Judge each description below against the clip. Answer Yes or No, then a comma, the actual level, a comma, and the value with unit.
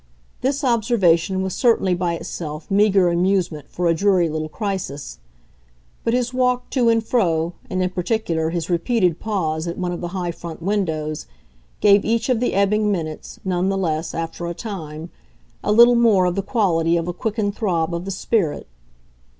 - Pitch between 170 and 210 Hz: Yes, medium, 185 Hz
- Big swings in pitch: No, average, 4.2 semitones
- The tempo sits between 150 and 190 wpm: Yes, average, 175 wpm